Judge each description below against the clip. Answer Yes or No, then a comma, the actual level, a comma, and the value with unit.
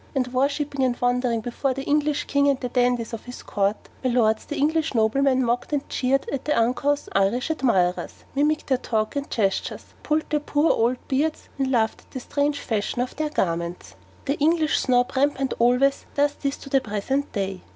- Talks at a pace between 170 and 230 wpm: Yes, average, 195 wpm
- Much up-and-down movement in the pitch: No, average, 3.4 semitones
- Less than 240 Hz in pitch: No, very high, 260 Hz